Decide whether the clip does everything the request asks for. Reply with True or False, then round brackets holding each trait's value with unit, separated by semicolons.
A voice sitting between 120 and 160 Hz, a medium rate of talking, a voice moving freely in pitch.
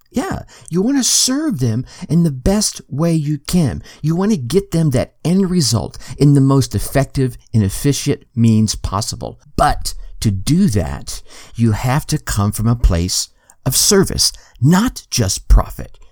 True (135 Hz; 165 wpm; 6.8 semitones)